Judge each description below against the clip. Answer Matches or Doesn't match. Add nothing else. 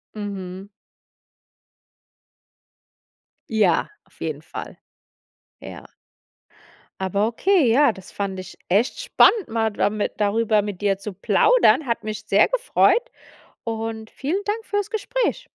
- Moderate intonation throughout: Doesn't match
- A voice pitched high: Matches